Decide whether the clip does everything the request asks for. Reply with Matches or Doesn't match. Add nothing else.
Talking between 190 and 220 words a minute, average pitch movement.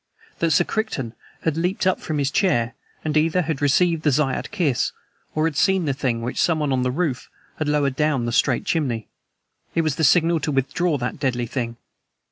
Matches